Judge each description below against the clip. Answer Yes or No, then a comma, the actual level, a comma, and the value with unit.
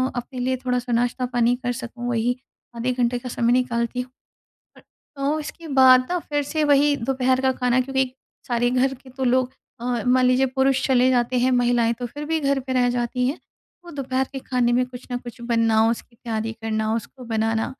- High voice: Yes, very high, 250 Hz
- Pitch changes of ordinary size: No, narrow, 1.6 semitones